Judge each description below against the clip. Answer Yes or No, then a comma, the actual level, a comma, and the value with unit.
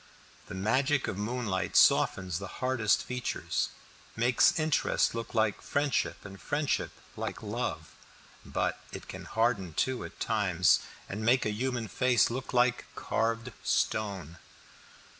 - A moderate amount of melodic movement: Yes, average, 4.0 semitones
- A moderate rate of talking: No, slow, 130 wpm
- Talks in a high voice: No, low, 115 Hz